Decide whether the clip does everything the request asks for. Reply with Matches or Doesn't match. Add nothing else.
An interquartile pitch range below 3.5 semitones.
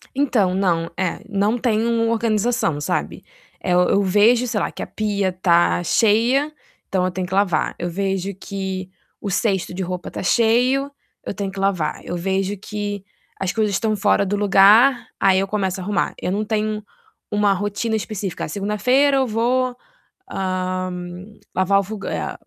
Matches